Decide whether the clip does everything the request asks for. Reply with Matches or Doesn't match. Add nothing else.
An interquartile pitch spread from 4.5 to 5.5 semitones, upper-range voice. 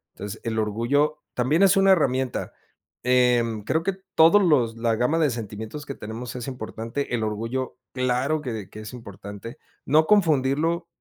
Doesn't match